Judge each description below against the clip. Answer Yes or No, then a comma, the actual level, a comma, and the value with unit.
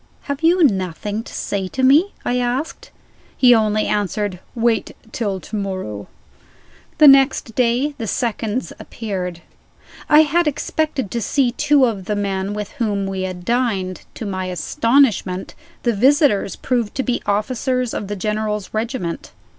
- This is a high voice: Yes, high, 220 Hz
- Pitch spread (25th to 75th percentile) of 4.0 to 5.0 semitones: Yes, average, 4.7 semitones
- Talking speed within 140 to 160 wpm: Yes, average, 150 wpm